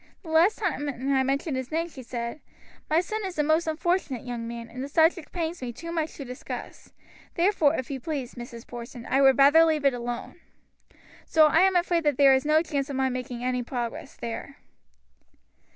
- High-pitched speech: Yes, very high, 280 Hz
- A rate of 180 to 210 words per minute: Yes, average, 200 wpm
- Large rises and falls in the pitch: No, average, 4.5 semitones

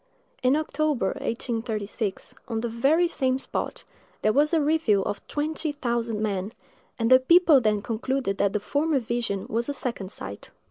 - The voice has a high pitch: Yes, high, 240 Hz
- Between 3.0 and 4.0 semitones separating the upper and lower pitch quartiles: No, average, 5.2 semitones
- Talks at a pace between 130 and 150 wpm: No, average, 165 wpm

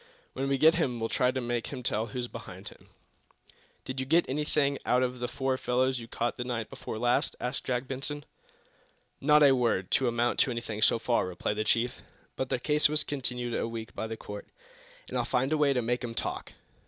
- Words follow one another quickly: Yes, fast, 215 wpm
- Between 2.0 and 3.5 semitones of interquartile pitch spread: Yes, narrow, 2.4 semitones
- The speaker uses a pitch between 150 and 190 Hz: No, low, 125 Hz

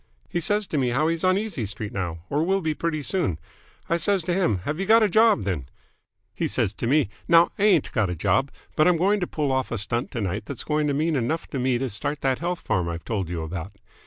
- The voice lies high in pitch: No, medium, 145 Hz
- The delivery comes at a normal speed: No, fast, 260 wpm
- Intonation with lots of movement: Yes, wide, 8.5 semitones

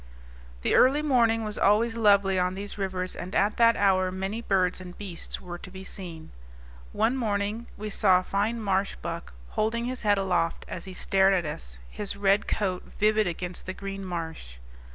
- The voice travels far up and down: No, narrow, 2.6 semitones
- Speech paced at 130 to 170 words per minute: No, average, 185 wpm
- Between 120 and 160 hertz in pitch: No, high, 195 Hz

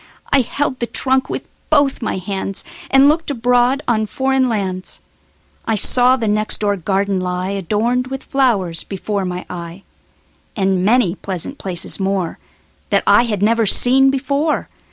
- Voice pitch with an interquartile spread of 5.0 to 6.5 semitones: Yes, average, 5.3 semitones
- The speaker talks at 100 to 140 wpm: Yes, slow, 135 wpm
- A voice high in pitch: Yes, high, 215 Hz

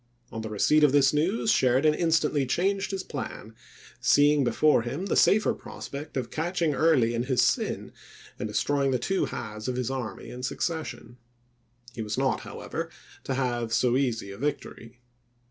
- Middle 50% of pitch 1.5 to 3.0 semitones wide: No, average, 4.3 semitones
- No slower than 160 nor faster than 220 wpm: Yes, average, 165 wpm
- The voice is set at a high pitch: No, low, 135 Hz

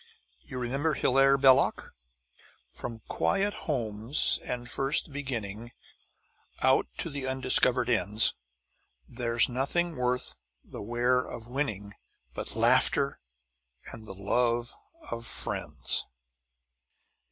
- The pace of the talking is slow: Yes, slow, 100 wpm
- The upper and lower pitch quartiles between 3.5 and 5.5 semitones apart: No, average, 2.8 semitones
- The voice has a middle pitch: No, low, 125 Hz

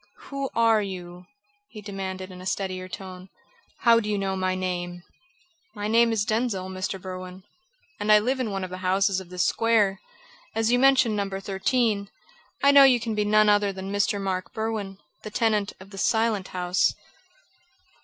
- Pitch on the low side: No, high, 200 Hz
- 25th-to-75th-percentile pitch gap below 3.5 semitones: Yes, average, 2.9 semitones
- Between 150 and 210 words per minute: Yes, average, 180 wpm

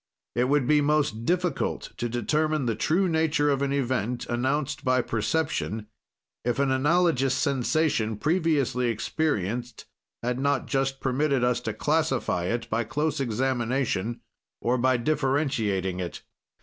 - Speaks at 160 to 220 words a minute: No, slow, 135 wpm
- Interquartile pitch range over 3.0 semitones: Yes, average, 3.9 semitones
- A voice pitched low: Yes, low, 130 Hz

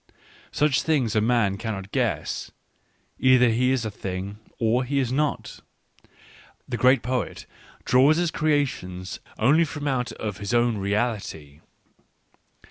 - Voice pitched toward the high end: No, low, 120 Hz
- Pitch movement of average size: Yes, average, 4.5 semitones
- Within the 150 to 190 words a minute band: No, slow, 135 wpm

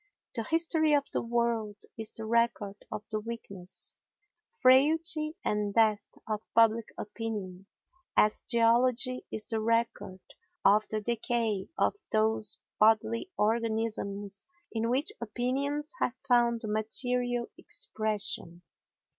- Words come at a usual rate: No, slow, 115 wpm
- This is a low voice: No, high, 225 Hz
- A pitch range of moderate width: No, narrow, 2.3 semitones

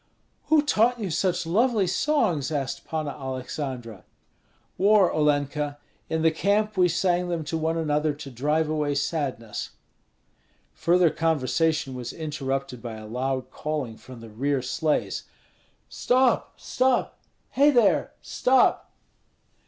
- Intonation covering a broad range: No, average, 5.0 semitones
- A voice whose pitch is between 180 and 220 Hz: No, medium, 155 Hz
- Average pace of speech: No, slow, 125 wpm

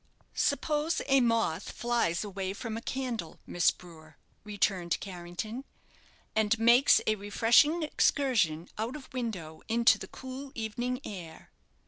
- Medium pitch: No, high, 220 Hz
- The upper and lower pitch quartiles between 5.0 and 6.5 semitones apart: Yes, wide, 5.5 semitones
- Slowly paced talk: Yes, slow, 125 wpm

